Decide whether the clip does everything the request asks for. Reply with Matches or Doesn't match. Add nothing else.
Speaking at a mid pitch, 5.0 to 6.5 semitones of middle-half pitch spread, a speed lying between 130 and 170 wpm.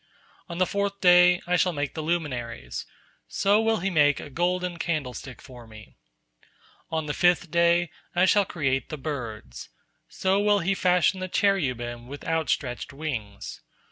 Matches